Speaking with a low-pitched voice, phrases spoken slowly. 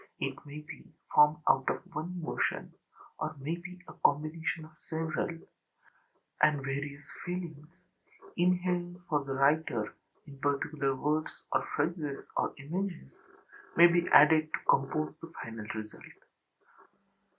No: medium, 155 Hz; slow, 130 wpm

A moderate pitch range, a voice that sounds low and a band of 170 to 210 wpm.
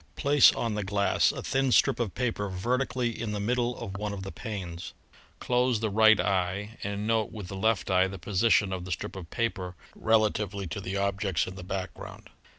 Yes: average, 3.1 semitones; low, 100 Hz; fast, 205 wpm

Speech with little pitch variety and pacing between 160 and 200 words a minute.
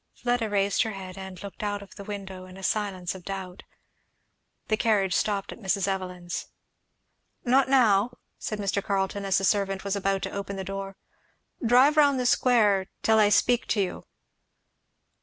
Yes: narrow, 2.2 semitones; average, 175 wpm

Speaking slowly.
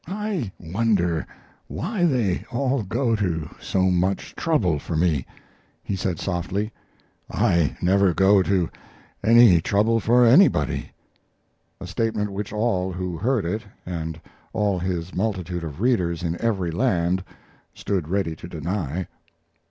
Yes: slow, 130 wpm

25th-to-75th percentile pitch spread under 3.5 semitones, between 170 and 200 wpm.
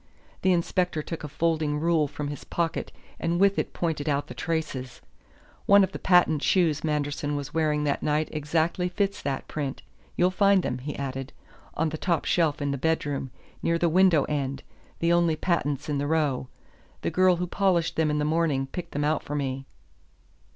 Yes: average, 2.9 semitones; average, 190 wpm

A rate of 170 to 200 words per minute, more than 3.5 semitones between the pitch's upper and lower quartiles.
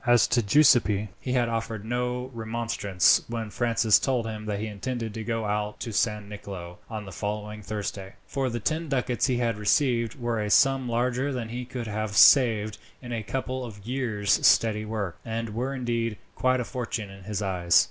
No: average, 190 wpm; average, 2.8 semitones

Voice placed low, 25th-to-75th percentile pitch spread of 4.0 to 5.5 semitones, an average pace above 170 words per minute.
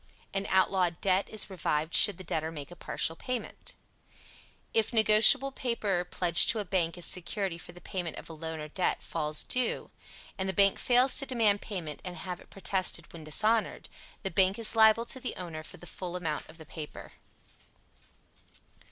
No: medium, 185 Hz; average, 4.4 semitones; average, 185 wpm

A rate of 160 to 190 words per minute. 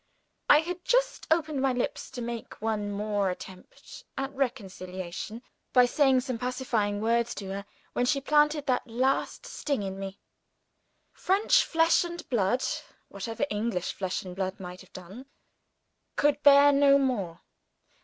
No: average, 145 wpm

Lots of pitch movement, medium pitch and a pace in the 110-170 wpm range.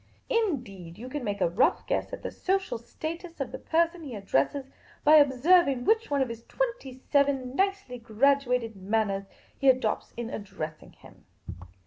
No: wide, 6.1 semitones; very high, 260 Hz; average, 160 wpm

